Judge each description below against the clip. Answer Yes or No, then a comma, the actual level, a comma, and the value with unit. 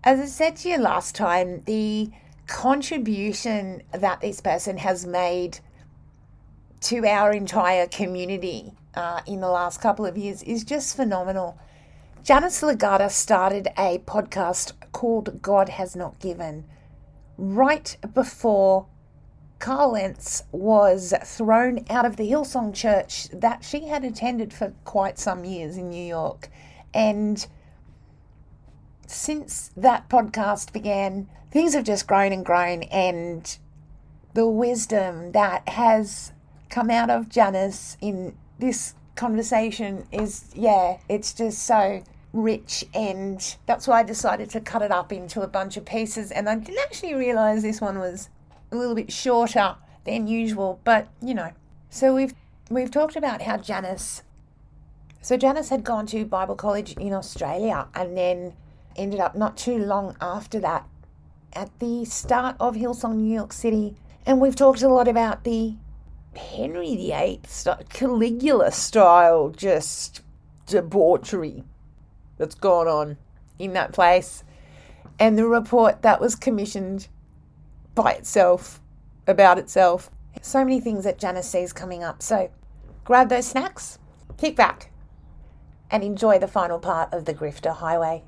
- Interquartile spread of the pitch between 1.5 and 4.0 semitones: No, average, 4.4 semitones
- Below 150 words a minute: Yes, average, 140 wpm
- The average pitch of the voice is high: Yes, high, 205 Hz